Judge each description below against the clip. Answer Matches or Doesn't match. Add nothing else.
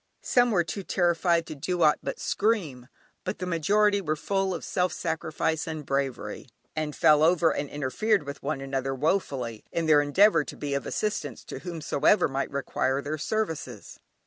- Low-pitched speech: Doesn't match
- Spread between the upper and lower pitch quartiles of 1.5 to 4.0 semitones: Doesn't match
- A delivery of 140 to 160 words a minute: Doesn't match